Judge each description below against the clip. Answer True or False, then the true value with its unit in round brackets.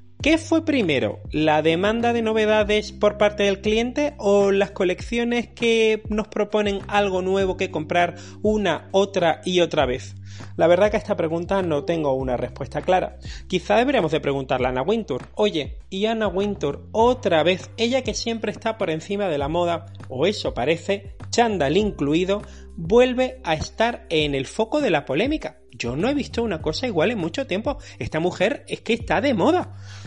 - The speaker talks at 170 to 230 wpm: True (180 wpm)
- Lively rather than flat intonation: True (5.7 semitones)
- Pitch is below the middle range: False (195 Hz)